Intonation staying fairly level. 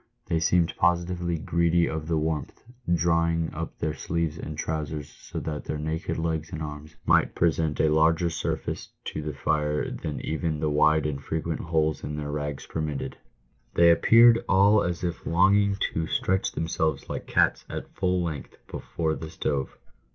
Yes: narrow, 1.8 semitones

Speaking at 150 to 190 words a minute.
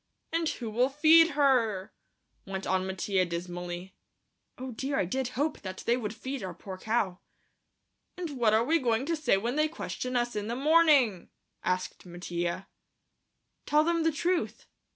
Yes: average, 160 wpm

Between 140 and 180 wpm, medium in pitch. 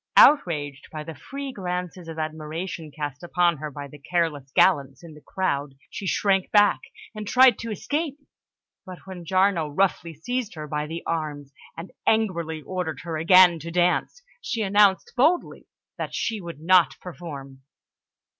Yes: average, 155 wpm; medium, 170 Hz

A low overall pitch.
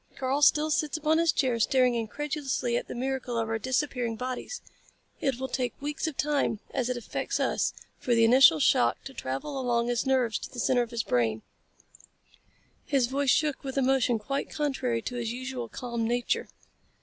No: very high, 255 Hz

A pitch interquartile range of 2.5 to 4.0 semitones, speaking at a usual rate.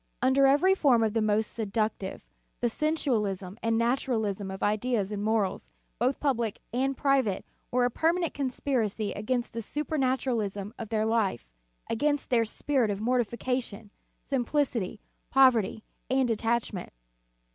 No: average, 3.7 semitones; slow, 125 wpm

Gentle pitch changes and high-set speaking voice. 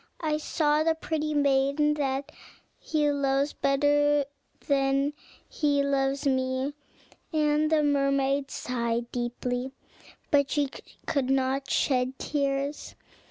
Yes: narrow, 1.6 semitones; very high, 280 Hz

